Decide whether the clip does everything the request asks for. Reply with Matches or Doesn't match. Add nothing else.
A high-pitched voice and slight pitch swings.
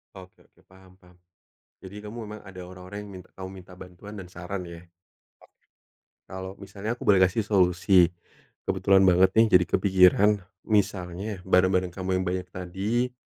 Doesn't match